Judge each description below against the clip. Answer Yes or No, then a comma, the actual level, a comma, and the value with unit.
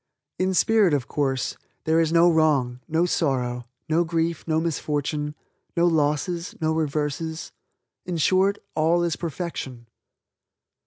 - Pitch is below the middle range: No, medium, 160 Hz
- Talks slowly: Yes, slow, 125 wpm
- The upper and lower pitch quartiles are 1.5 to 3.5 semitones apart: Yes, narrow, 2.5 semitones